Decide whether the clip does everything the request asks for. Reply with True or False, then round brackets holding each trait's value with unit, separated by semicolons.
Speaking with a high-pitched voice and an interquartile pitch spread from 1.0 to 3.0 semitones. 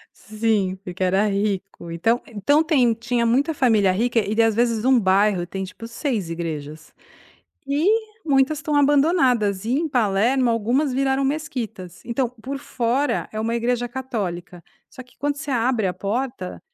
False (230 Hz; 5.0 semitones)